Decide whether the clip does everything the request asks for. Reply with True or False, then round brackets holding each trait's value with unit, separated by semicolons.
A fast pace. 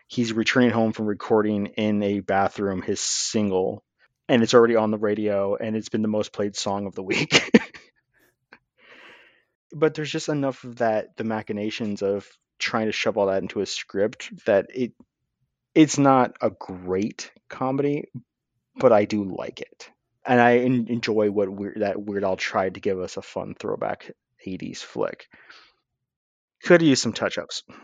False (165 wpm)